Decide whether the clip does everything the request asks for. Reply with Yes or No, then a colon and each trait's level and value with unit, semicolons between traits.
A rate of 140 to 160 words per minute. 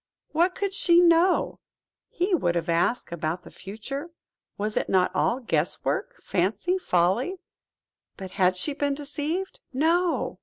Yes: average, 145 wpm